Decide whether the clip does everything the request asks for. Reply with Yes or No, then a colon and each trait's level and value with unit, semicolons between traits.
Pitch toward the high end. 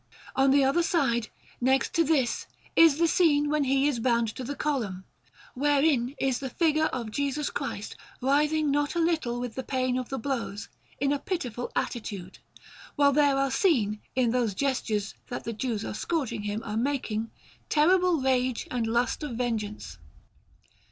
Yes: very high, 265 Hz